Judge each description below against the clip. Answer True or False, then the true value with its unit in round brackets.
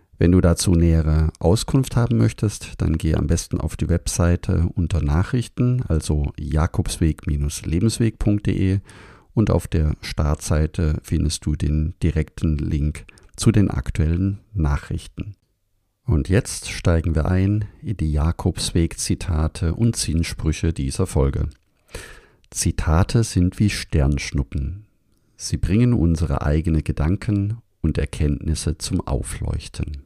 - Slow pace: True (110 wpm)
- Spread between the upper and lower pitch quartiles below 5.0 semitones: True (4.4 semitones)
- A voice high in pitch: False (85 Hz)